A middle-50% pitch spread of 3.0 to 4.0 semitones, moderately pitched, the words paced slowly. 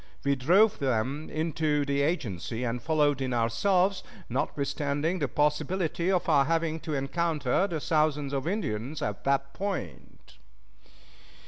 Yes: average, 3.5 semitones; medium, 150 Hz; slow, 130 wpm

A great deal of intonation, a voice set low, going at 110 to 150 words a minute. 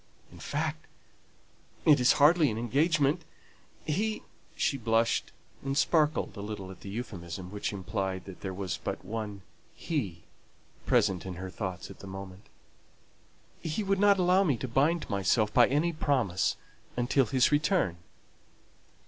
Yes: wide, 7.7 semitones; low, 115 Hz; average, 140 wpm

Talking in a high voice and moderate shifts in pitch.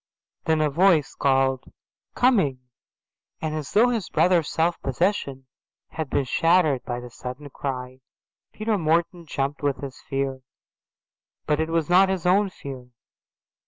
No: medium, 155 Hz; average, 4.9 semitones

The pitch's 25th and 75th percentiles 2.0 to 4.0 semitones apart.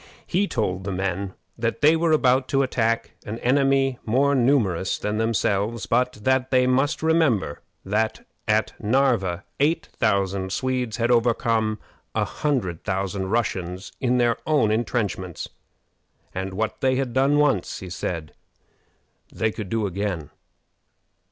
No: average, 5.0 semitones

